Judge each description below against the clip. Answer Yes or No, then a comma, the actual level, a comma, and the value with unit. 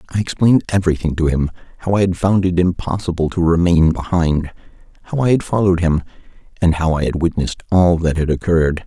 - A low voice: Yes, very low, 85 Hz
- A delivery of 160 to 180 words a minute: No, average, 190 wpm